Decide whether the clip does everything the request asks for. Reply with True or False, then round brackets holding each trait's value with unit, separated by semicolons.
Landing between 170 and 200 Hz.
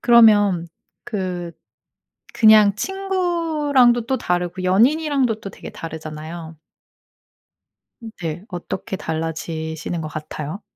True (190 Hz)